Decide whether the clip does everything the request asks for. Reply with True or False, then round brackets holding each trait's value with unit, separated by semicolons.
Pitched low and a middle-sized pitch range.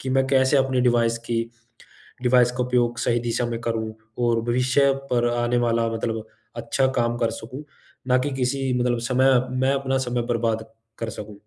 False (120 Hz; 2.0 semitones)